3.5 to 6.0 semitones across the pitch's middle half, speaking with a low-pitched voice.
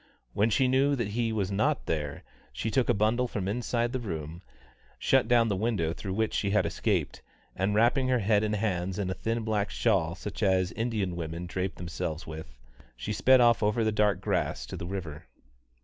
Yes: average, 4.3 semitones; low, 105 Hz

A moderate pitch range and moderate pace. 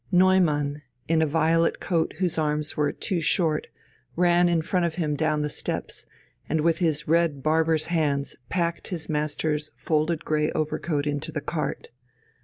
No: narrow, 2.0 semitones; average, 165 wpm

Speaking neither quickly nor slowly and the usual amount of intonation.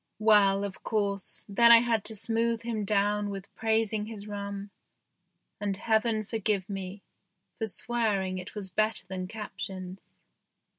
No: average, 145 wpm; narrow, 2.1 semitones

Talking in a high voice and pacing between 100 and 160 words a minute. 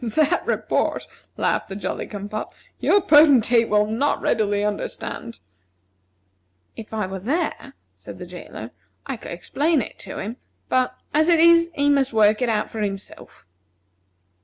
Yes: high, 230 Hz; average, 155 wpm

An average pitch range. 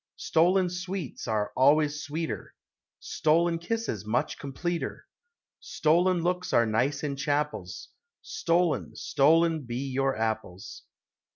Yes: average, 5.0 semitones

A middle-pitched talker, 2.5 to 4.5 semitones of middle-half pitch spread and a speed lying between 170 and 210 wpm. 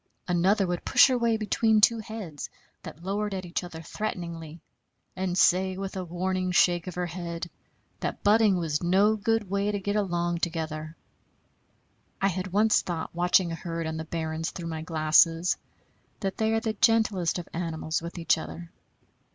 Yes: medium, 180 Hz; average, 3.3 semitones; average, 175 wpm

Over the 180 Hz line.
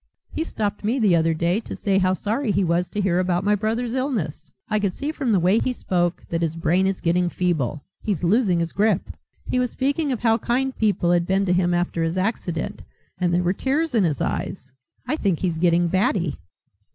Yes: high, 190 Hz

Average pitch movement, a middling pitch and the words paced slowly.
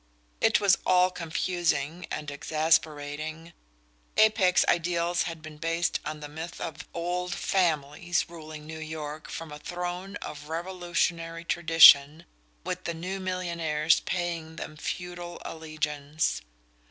No: narrow, 2.2 semitones; medium, 165 Hz; slow, 120 wpm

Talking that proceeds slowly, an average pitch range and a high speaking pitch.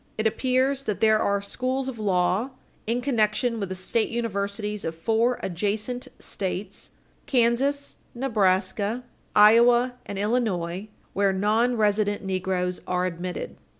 Yes: slow, 120 wpm; average, 3.9 semitones; high, 215 Hz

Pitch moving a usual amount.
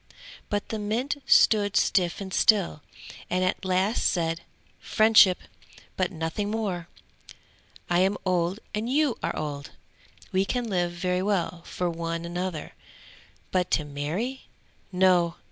Yes: average, 3.2 semitones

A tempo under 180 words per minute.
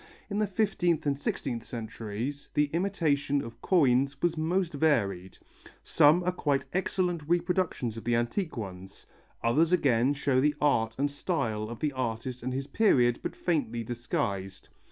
Yes: average, 155 wpm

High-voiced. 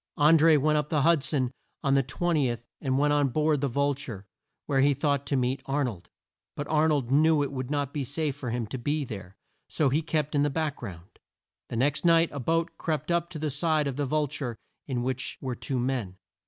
No: medium, 140 Hz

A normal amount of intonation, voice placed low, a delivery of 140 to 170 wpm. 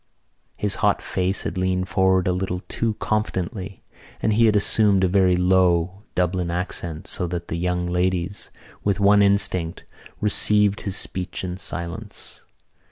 No: narrow, 2.1 semitones; very low, 95 Hz; average, 155 wpm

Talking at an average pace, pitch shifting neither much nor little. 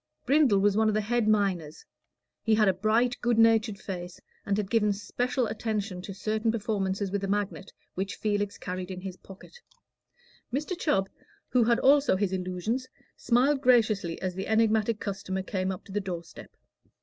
Yes: average, 175 wpm; average, 3.1 semitones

